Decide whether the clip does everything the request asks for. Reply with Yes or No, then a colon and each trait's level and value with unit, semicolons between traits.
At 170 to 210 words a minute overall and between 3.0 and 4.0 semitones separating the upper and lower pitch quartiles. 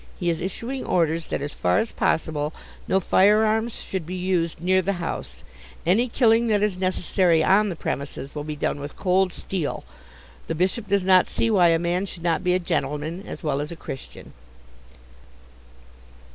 Yes: average, 180 wpm; average, 3.4 semitones